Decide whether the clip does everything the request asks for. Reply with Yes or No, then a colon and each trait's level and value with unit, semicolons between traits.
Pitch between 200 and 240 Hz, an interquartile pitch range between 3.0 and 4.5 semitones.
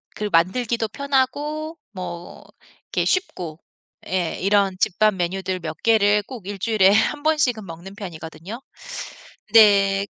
Yes: high, 205 Hz; average, 4.2 semitones